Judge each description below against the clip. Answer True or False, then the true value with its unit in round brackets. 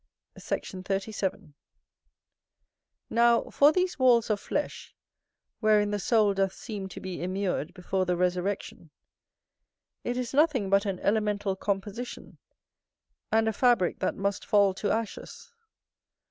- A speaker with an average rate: False (125 wpm)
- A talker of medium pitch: False (205 Hz)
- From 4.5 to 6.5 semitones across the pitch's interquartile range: False (3.4 semitones)